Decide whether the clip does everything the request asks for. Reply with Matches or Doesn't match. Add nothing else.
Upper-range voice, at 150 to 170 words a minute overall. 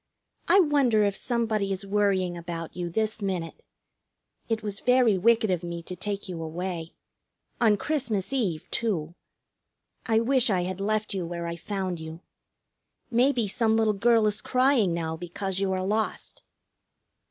Matches